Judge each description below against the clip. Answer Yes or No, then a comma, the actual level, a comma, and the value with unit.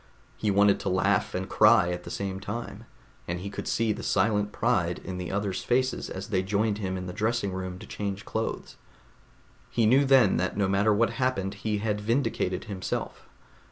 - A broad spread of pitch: No, average, 2.7 semitones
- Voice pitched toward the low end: Yes, low, 100 Hz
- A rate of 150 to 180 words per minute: No, average, 190 wpm